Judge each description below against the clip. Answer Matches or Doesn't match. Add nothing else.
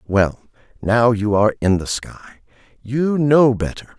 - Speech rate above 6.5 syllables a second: Doesn't match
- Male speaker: Matches